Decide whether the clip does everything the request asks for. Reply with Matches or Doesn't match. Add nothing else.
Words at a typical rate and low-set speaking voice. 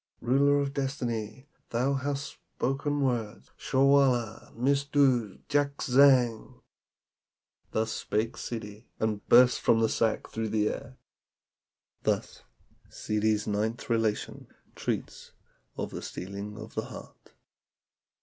Doesn't match